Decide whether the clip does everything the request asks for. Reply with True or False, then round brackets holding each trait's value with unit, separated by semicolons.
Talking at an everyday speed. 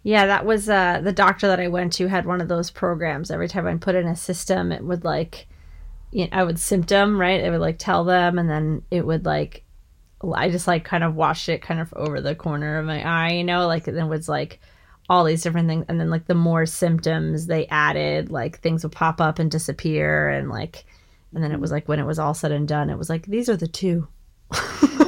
False (245 wpm)